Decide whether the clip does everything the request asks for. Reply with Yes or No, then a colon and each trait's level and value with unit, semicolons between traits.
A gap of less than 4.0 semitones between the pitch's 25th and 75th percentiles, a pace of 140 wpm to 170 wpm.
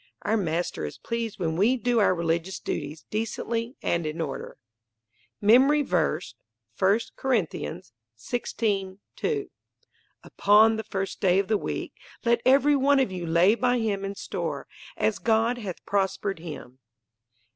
No: average, 5.3 semitones; average, 145 wpm